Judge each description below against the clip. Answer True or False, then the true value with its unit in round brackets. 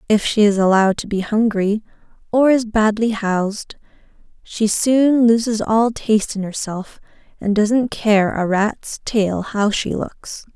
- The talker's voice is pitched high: True (215 Hz)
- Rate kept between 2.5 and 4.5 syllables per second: True (4.0 syllables/s)